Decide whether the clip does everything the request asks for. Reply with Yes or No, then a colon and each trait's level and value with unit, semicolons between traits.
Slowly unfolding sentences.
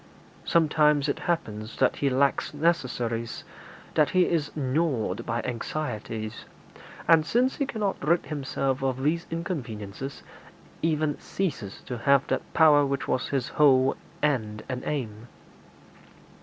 Yes: slow, 130 wpm